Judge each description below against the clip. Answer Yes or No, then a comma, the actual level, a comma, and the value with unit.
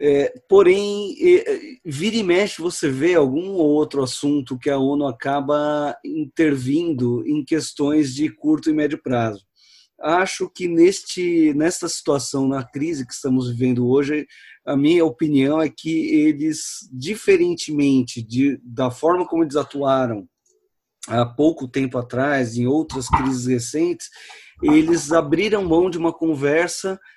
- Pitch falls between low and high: Yes, medium, 155 Hz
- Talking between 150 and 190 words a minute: No, average, 135 wpm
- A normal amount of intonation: No, wide, 7.9 semitones